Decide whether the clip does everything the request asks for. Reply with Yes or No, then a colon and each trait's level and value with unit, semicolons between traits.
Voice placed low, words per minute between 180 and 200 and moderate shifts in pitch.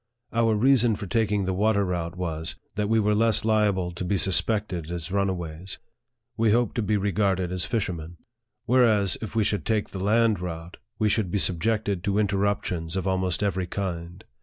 Yes: low, 100 Hz; average, 185 wpm; average, 3.1 semitones